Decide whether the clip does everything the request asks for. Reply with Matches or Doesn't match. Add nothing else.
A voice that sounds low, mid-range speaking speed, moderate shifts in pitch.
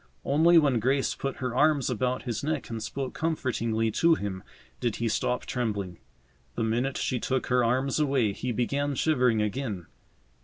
Matches